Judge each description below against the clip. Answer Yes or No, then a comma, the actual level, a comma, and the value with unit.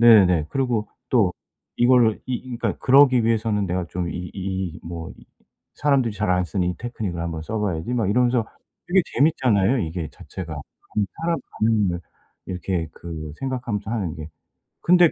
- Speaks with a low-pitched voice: Yes, low, 105 Hz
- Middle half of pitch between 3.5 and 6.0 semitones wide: Yes, wide, 5.6 semitones